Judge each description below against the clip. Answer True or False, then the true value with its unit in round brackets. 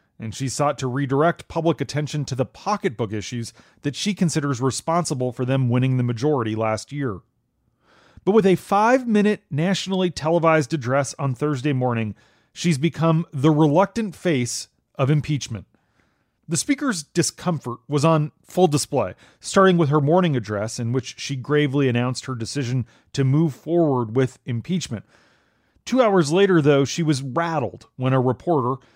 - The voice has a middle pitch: True (145 Hz)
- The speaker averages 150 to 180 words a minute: True (155 wpm)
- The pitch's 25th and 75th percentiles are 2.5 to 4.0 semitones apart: False (5.0 semitones)